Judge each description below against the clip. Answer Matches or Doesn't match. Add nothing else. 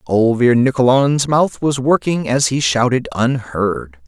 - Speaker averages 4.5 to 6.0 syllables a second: Doesn't match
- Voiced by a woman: Doesn't match